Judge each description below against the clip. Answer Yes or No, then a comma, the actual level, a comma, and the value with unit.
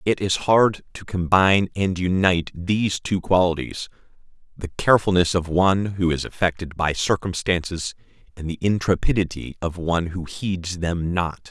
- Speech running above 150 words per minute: No, average, 145 wpm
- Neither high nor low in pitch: No, very low, 90 Hz